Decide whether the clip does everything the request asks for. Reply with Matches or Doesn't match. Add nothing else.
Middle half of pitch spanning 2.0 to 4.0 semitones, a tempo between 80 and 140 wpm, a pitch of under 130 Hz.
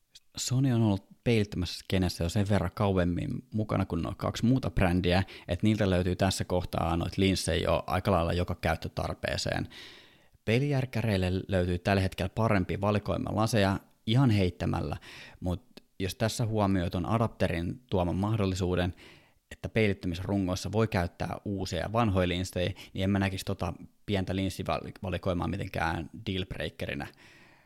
Matches